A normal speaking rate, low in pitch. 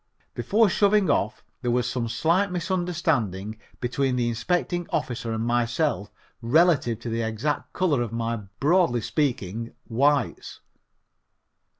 No: slow, 120 wpm; low, 125 Hz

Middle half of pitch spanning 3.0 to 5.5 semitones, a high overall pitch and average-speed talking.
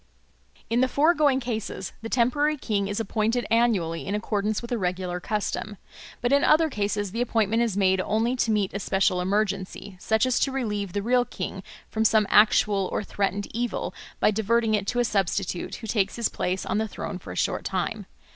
Yes: average, 3.3 semitones; high, 215 Hz; average, 195 wpm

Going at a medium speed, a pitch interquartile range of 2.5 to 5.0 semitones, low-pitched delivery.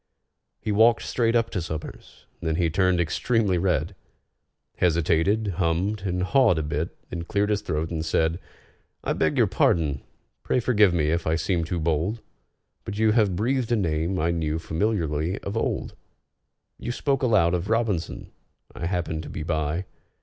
Yes: average, 160 wpm; average, 4.7 semitones; very low, 90 Hz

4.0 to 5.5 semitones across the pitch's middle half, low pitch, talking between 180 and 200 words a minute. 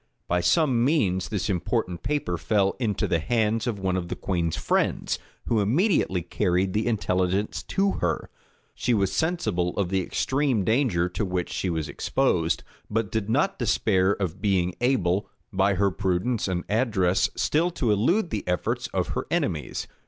No: average, 4.6 semitones; low, 100 Hz; average, 165 wpm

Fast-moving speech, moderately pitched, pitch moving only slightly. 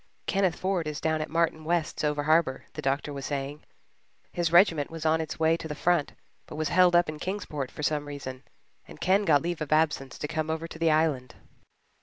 Yes: fast, 215 wpm; medium, 155 Hz; narrow, 2.3 semitones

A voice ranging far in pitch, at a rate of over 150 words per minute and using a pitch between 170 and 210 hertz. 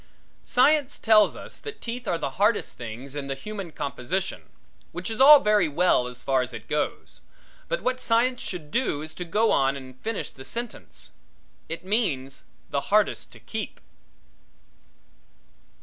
Yes: wide, 9.0 semitones; average, 165 wpm; medium, 185 Hz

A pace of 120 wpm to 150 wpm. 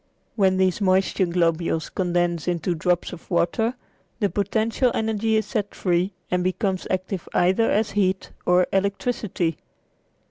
Yes: slow, 135 wpm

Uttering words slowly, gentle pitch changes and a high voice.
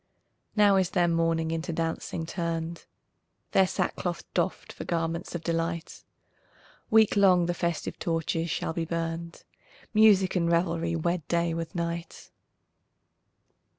No: slow, 125 wpm; narrow, 1.1 semitones; medium, 170 Hz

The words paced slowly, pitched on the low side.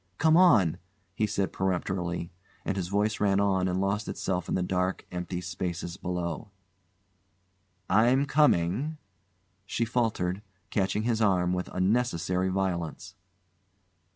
Yes: slow, 125 wpm; very low, 95 Hz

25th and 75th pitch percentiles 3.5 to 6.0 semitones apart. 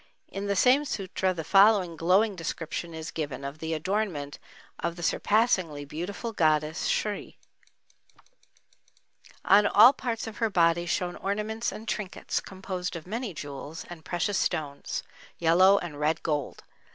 Yes: average, 4.3 semitones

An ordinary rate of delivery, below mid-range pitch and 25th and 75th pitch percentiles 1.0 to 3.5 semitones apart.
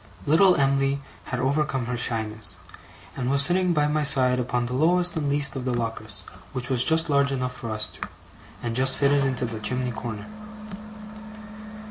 Yes: average, 175 wpm; low, 130 Hz; average, 2.9 semitones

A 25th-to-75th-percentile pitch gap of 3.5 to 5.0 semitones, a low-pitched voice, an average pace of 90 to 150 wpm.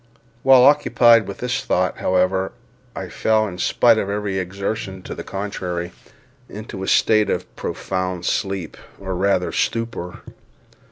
No: average, 3.1 semitones; low, 100 Hz; slow, 135 wpm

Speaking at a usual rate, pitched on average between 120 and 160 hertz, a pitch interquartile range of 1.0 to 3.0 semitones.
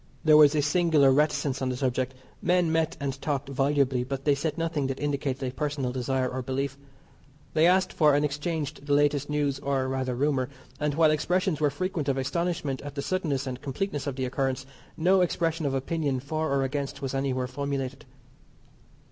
Yes: average, 190 wpm; medium, 140 Hz; narrow, 2.5 semitones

